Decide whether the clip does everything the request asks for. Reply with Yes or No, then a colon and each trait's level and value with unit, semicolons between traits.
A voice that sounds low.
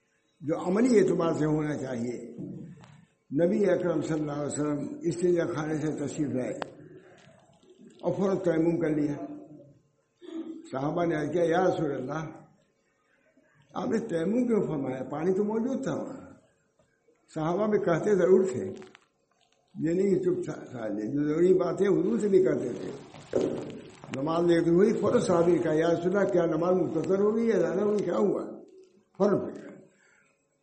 No: medium, 170 Hz